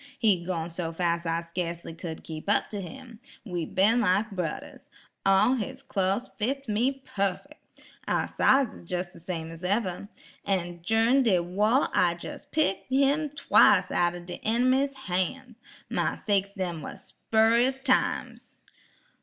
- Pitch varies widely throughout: Yes, wide, 6.2 semitones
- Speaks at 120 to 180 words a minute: Yes, average, 150 wpm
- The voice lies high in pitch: Yes, high, 200 Hz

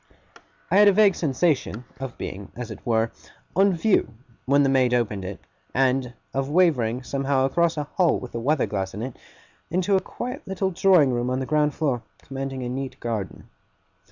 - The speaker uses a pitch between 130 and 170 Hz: Yes, low, 135 Hz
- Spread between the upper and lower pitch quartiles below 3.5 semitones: No, wide, 5.5 semitones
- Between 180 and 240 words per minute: Yes, average, 185 wpm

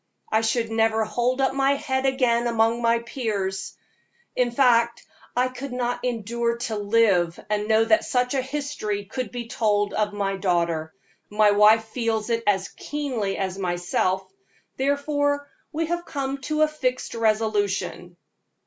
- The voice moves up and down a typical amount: Yes, average, 3.8 semitones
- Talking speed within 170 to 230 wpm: No, average, 155 wpm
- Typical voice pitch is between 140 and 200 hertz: No, high, 230 Hz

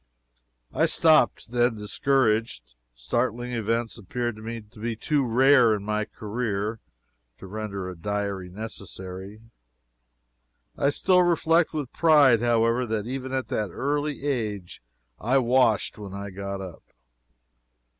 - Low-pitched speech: Yes, low, 115 Hz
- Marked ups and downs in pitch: No, average, 4.0 semitones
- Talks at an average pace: No, slow, 125 wpm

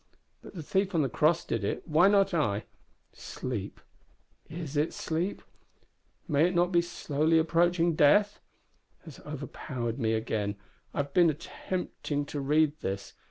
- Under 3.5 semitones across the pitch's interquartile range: No, average, 4.0 semitones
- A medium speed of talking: Yes, average, 150 wpm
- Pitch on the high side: No, medium, 155 Hz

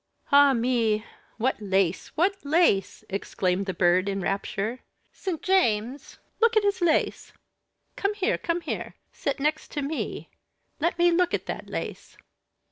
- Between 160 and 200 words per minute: No, average, 145 wpm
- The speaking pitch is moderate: No, very high, 275 Hz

